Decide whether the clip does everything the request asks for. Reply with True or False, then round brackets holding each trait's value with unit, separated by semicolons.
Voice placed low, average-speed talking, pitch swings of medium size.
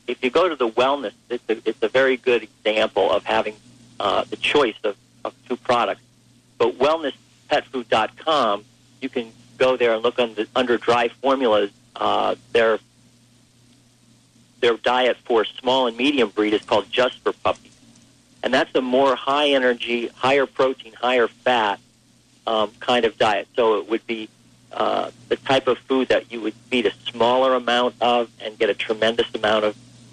False (120 Hz; 170 wpm; 1.8 semitones)